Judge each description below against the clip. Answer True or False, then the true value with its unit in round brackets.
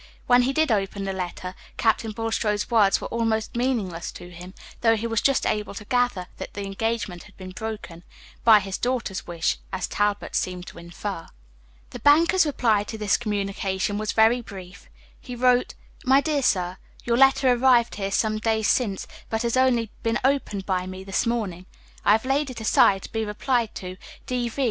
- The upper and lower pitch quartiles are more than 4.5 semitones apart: False (3.8 semitones)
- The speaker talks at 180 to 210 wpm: True (185 wpm)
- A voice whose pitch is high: True (220 Hz)